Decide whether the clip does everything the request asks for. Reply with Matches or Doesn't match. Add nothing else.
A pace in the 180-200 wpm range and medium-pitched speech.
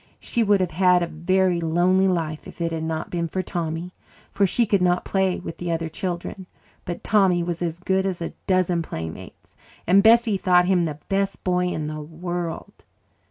Matches